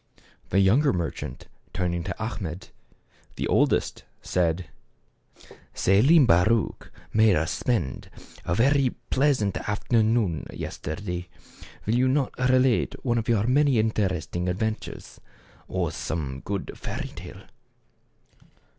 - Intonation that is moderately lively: No, wide, 5.7 semitones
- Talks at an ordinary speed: No, slow, 110 wpm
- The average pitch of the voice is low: Yes, low, 105 Hz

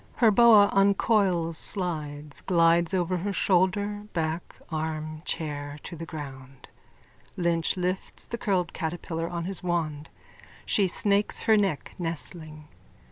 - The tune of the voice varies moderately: Yes, average, 3.7 semitones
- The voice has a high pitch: No, medium, 170 Hz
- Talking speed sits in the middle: No, slow, 125 wpm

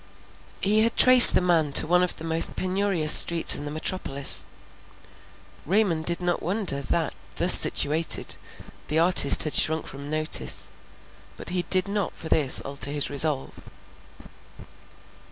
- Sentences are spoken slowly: No, average, 145 wpm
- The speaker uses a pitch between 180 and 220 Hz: No, medium, 165 Hz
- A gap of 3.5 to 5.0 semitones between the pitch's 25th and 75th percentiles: Yes, average, 3.8 semitones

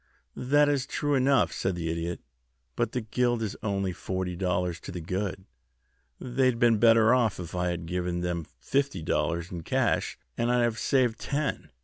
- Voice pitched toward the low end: Yes, low, 100 Hz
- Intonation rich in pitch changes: Yes, wide, 6.0 semitones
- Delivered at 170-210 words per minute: Yes, average, 185 wpm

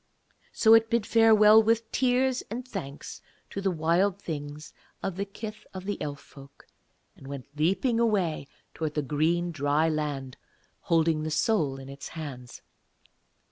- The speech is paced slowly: No, average, 145 wpm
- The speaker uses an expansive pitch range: Yes, wide, 6.7 semitones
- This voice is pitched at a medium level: Yes, medium, 165 Hz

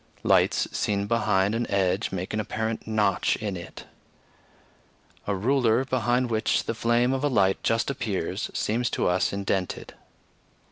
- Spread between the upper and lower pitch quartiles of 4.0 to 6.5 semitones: No, average, 3.3 semitones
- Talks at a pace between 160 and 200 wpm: No, average, 145 wpm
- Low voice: Yes, low, 110 Hz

